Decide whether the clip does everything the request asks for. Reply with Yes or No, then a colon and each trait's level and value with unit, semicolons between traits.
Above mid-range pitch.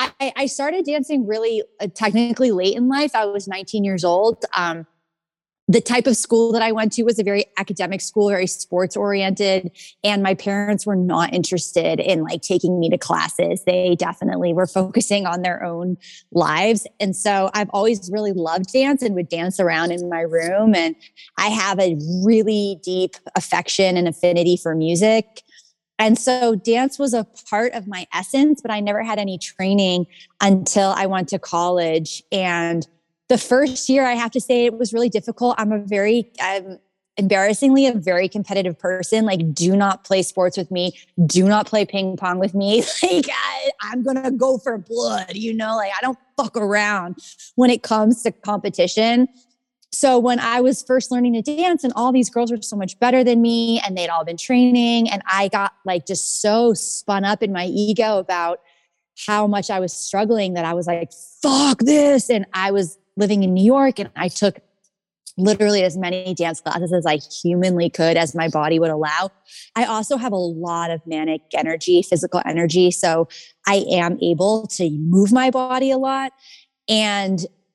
Yes: high, 200 Hz